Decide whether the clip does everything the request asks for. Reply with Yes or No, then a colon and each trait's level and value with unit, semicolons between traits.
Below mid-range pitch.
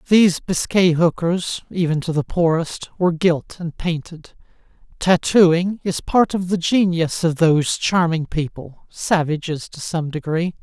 No: medium, 170 Hz